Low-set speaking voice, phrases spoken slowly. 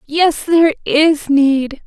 No: very high, 300 Hz; slow, 130 wpm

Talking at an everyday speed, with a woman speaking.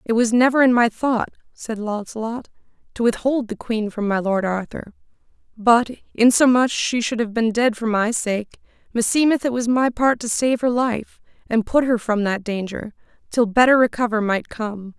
Yes: average, 185 wpm; female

